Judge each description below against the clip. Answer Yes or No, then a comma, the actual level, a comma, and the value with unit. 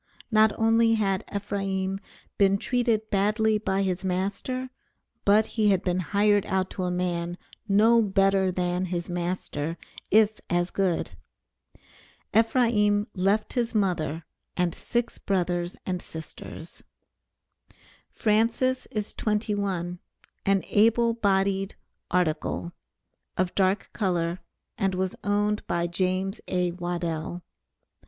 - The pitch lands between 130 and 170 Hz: No, high, 195 Hz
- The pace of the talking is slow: Yes, slow, 115 wpm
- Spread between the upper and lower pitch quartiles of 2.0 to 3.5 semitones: Yes, average, 3.0 semitones